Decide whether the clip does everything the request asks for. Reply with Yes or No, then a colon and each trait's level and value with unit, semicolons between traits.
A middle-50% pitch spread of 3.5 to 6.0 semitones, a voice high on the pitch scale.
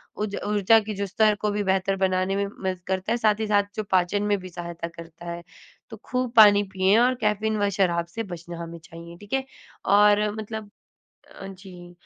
No: average, 2.9 semitones; high, 200 Hz